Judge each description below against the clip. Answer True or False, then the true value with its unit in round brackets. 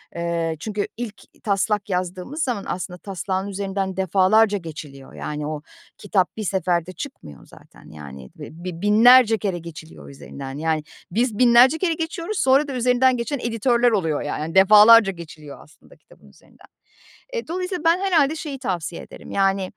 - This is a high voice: True (200 Hz)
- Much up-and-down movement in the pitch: True (6.4 semitones)